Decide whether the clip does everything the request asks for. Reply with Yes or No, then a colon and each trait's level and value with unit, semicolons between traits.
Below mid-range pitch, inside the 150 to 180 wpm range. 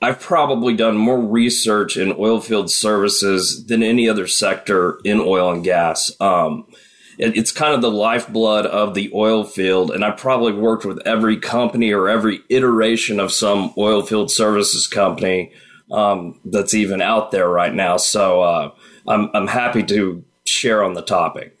Yes: low, 105 Hz; average, 170 wpm